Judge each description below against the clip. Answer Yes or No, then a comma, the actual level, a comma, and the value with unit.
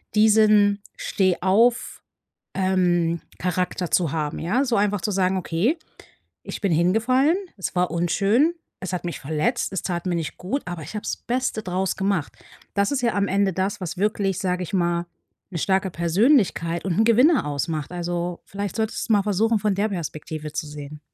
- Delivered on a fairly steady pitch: No, average, 3.6 semitones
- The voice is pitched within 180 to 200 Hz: Yes, high, 190 Hz